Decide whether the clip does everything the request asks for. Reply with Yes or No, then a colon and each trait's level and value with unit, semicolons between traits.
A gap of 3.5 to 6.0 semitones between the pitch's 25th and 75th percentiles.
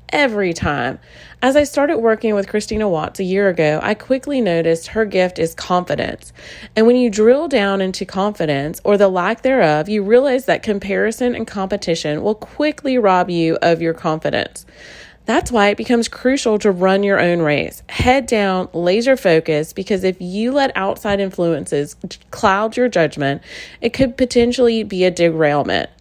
Yes: wide, 5.4 semitones